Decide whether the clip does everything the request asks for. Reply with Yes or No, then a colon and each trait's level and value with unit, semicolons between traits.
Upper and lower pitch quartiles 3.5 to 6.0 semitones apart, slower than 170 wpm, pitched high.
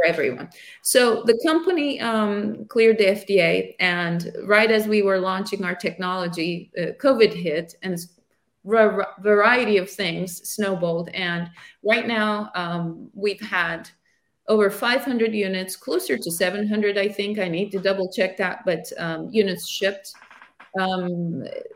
No: average, 3.1 semitones; average, 140 wpm; high, 200 Hz